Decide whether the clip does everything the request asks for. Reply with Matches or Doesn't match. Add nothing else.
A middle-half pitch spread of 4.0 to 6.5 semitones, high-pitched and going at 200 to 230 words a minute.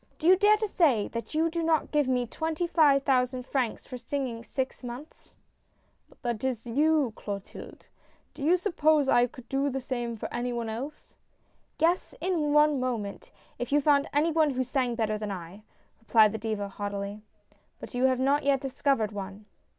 Matches